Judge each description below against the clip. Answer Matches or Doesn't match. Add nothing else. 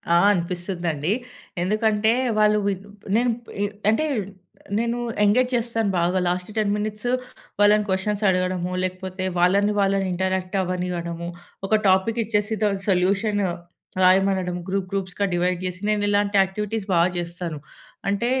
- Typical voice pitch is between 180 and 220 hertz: Matches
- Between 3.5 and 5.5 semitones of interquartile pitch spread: Doesn't match